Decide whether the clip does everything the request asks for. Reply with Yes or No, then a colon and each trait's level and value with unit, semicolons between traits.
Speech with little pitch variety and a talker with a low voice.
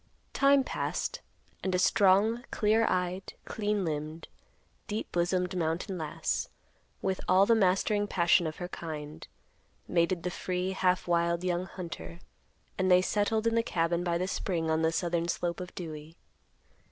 No: narrow, 2.3 semitones; medium, 180 Hz